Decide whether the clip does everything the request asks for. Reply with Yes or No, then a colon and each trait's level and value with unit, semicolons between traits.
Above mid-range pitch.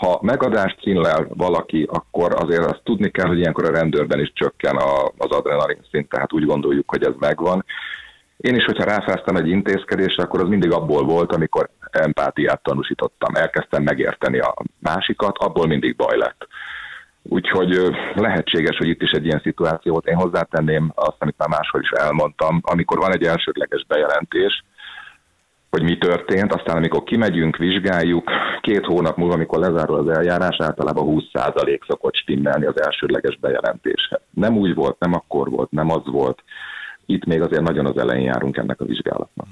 Yes: very high, 275 Hz